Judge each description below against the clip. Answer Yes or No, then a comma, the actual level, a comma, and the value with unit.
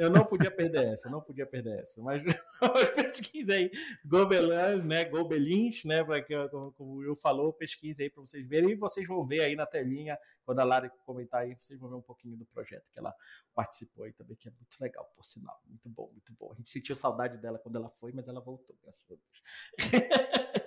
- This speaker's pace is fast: Yes, fast, 220 wpm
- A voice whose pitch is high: No, medium, 140 Hz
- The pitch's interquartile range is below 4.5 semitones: No, average, 5.0 semitones